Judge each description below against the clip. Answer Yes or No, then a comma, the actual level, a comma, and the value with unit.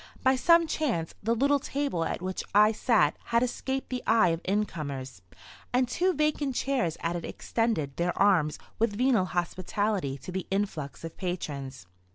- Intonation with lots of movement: Yes, wide, 7.3 semitones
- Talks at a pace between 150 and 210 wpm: Yes, average, 165 wpm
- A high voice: Yes, high, 205 Hz